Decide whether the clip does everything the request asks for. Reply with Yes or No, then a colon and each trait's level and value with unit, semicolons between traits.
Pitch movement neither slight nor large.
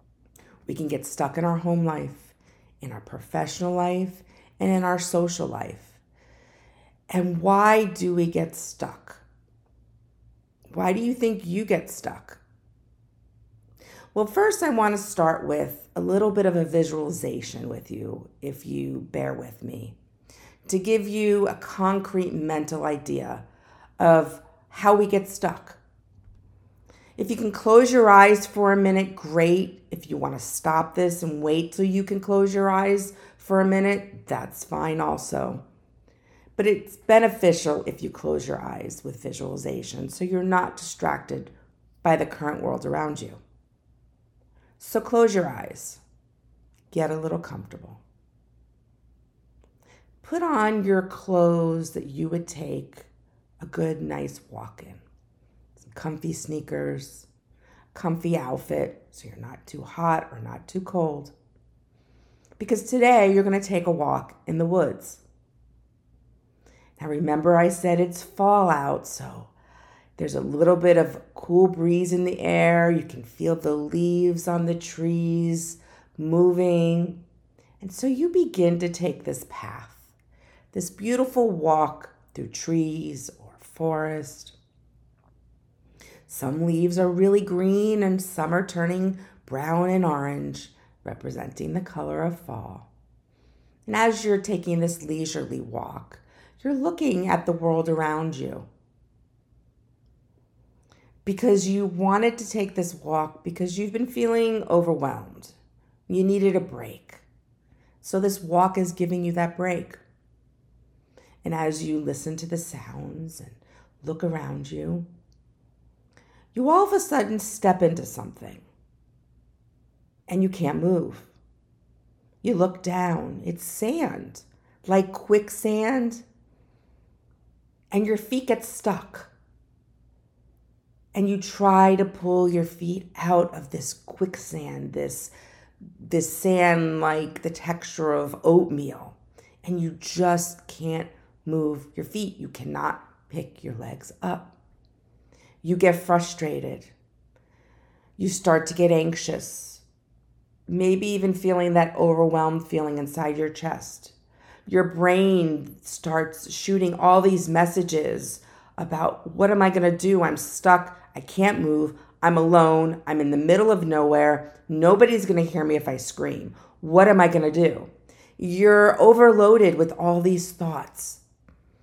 Yes: average, 4.3 semitones